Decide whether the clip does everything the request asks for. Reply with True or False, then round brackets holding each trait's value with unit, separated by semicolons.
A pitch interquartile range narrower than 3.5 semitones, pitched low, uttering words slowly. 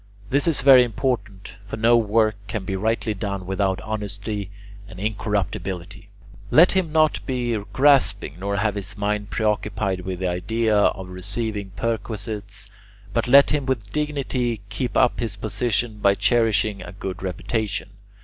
False (3.1 semitones; 105 Hz; 150 wpm)